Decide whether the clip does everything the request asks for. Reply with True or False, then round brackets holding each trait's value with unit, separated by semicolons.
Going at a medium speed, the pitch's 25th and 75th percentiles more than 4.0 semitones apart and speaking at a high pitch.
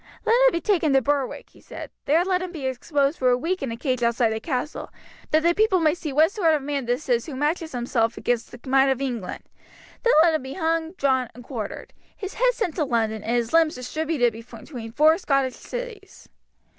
False (225 wpm; 5.2 semitones; 280 Hz)